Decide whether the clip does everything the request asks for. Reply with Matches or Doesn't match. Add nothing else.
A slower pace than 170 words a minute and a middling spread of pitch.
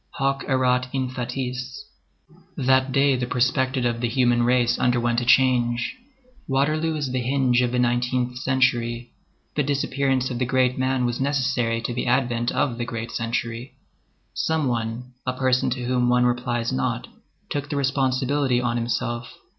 Doesn't match